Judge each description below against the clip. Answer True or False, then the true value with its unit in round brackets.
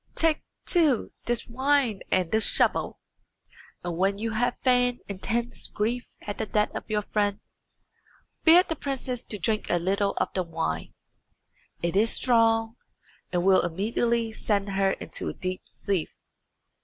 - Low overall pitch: False (215 Hz)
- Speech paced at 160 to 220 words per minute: False (150 wpm)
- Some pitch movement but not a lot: True (3.8 semitones)